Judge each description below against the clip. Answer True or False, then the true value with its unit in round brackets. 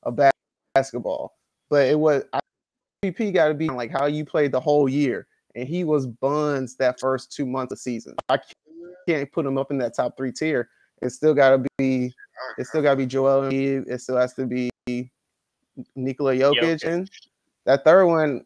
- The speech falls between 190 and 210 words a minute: True (200 wpm)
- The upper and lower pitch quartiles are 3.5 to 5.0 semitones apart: False (2.8 semitones)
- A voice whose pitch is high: False (135 Hz)